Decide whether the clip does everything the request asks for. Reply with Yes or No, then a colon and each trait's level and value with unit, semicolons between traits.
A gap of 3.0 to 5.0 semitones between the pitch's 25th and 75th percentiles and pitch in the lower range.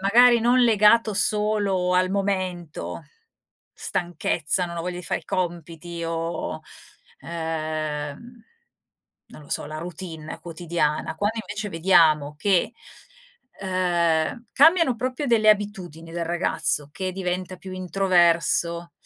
No: average, 3.6 semitones; medium, 180 Hz